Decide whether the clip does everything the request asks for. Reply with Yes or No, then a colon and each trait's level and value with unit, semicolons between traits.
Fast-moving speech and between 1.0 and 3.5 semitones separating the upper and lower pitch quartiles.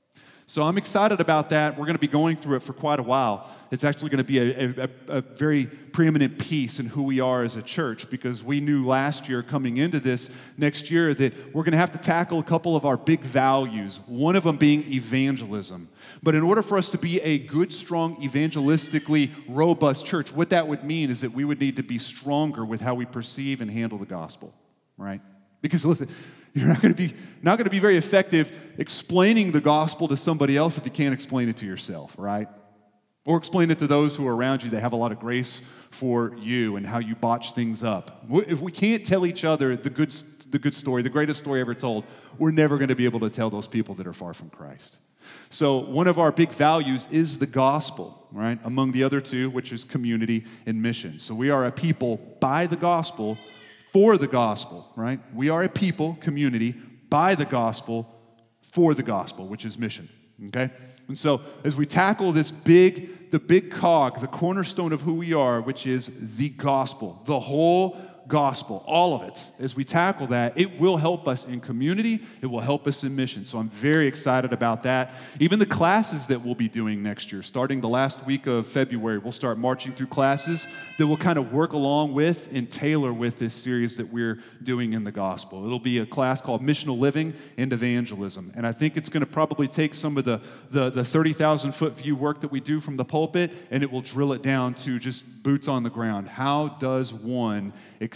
No: fast, 220 wpm; average, 4.4 semitones